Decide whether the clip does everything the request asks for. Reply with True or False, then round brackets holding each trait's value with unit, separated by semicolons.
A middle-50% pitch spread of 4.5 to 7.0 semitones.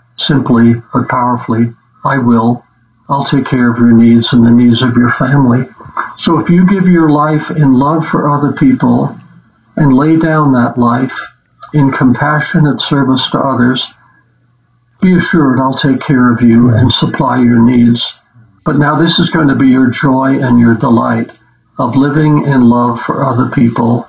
False (3.4 semitones)